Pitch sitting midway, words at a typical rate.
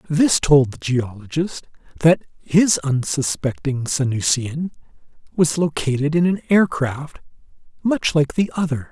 No: medium, 150 Hz; slow, 115 wpm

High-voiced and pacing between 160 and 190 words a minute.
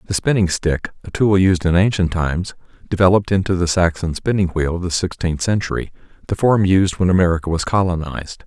No: very low, 90 Hz; average, 185 wpm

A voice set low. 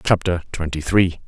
Yes: very low, 85 Hz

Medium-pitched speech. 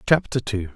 No: low, 105 Hz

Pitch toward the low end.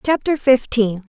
No: high, 245 Hz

